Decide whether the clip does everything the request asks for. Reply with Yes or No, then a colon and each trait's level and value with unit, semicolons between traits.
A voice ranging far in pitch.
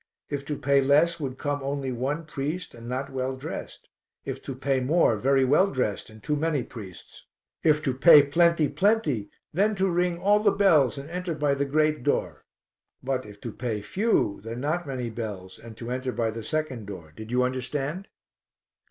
No: average, 4.2 semitones